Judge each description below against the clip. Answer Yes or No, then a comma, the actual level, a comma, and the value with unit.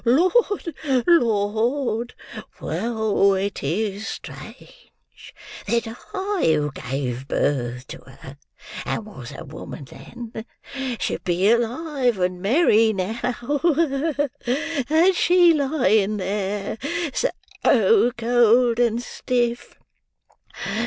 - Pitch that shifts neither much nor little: Yes, average, 4.9 semitones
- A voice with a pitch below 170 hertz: No, high, 225 Hz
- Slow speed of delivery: Yes, slow, 90 wpm